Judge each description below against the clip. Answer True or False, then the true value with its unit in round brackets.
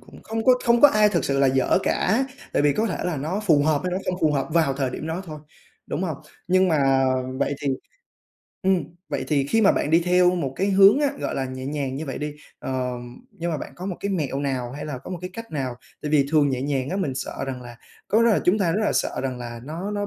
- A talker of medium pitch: True (155 Hz)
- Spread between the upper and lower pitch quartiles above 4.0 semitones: True (5.5 semitones)